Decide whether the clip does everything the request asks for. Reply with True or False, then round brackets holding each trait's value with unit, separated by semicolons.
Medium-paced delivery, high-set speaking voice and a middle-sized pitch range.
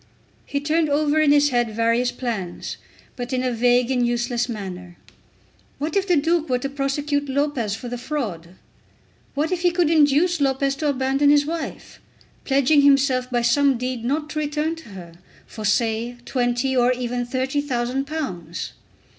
True (170 wpm; 265 Hz; 3.4 semitones)